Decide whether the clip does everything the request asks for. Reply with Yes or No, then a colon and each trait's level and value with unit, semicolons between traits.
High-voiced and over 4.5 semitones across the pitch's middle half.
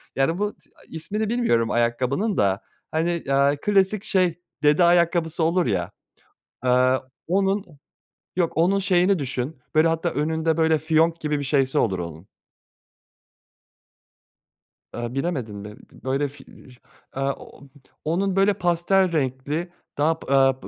No: medium, 160 Hz; average, 5.0 semitones